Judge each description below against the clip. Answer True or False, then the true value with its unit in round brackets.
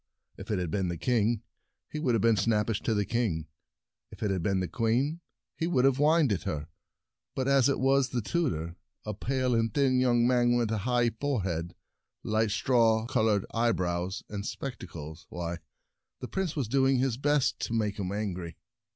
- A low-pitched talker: True (115 Hz)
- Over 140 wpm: True (190 wpm)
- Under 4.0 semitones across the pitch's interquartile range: False (4.8 semitones)